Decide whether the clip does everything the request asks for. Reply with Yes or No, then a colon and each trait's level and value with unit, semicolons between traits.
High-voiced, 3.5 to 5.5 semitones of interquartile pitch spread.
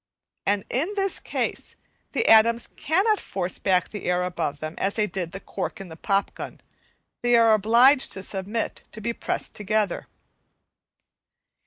Yes: high, 210 Hz; average, 3.8 semitones